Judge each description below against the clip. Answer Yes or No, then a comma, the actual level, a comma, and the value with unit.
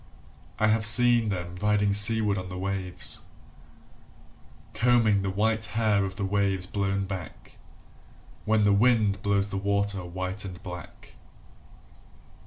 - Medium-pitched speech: No, low, 100 Hz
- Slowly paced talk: Yes, slow, 130 wpm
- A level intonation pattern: Yes, narrow, 2.0 semitones